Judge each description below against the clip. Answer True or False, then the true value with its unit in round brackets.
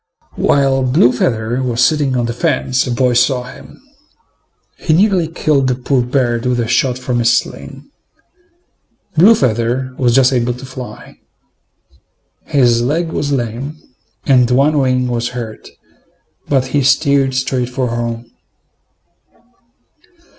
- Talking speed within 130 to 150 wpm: True (135 wpm)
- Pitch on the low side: True (130 Hz)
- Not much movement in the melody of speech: True (2.3 semitones)